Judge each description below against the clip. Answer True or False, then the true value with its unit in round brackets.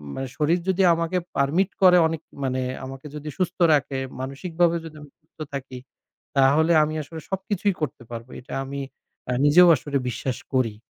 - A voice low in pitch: False (150 Hz)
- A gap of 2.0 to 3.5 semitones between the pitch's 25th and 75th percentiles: False (4.3 semitones)